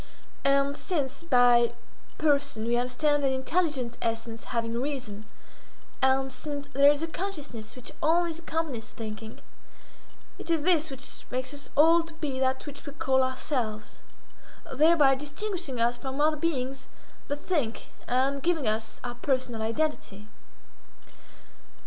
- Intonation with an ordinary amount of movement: Yes, average, 3.9 semitones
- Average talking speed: No, slow, 130 wpm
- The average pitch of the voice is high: Yes, very high, 270 Hz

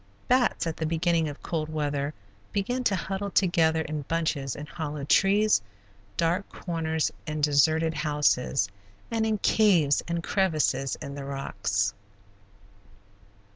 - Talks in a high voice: No, medium, 160 Hz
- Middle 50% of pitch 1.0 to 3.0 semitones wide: No, average, 4.1 semitones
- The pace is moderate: No, slow, 130 wpm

